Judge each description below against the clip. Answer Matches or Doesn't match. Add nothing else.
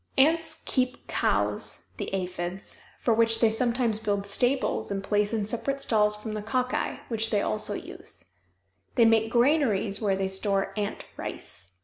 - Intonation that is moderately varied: Matches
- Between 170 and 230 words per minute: Doesn't match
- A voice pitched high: Matches